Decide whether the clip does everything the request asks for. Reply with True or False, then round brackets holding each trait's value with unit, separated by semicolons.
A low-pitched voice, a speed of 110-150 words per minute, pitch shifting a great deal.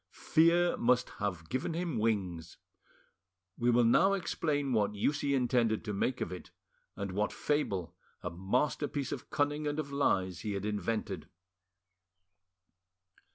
True (120 Hz; 140 wpm; 6.5 semitones)